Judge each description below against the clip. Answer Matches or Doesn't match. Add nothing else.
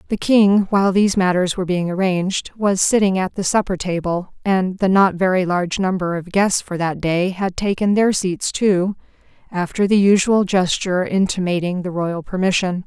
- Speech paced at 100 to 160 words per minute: Doesn't match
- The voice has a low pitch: Doesn't match